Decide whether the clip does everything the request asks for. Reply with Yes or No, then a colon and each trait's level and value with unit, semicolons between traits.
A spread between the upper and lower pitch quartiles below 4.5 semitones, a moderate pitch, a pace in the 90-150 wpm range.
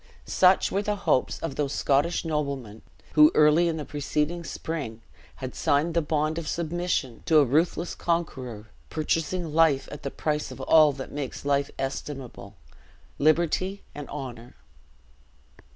Yes: average, 3.3 semitones; medium, 150 Hz; average, 145 wpm